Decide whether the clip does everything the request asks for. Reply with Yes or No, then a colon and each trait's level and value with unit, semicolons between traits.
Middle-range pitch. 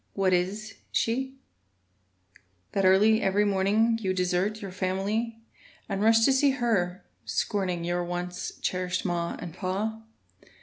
No: high, 195 Hz